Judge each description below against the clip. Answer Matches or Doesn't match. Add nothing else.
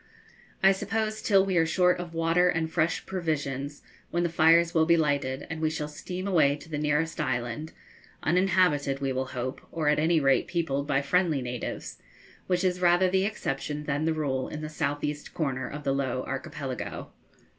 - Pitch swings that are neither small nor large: Matches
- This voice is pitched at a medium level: Matches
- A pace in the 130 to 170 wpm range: Doesn't match